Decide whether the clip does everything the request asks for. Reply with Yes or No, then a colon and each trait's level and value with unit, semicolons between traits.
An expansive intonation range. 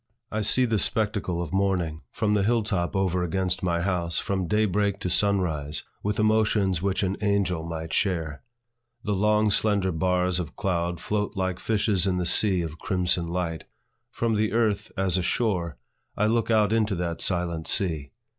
No: average, 3.2 semitones